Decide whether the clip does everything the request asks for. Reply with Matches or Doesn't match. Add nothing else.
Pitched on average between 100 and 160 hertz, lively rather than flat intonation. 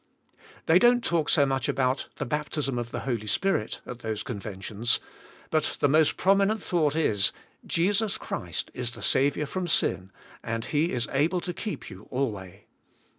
Matches